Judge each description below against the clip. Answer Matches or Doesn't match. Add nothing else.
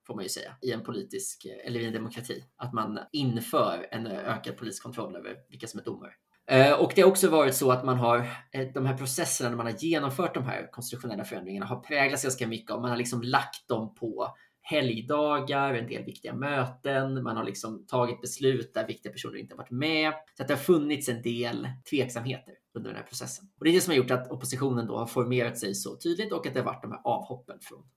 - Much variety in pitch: Doesn't match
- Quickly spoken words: Matches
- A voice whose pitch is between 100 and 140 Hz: Matches